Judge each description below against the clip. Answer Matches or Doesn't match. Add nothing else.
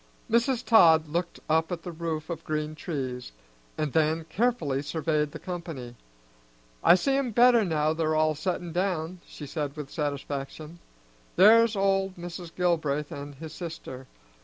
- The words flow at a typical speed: Matches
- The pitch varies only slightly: Doesn't match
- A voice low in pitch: Doesn't match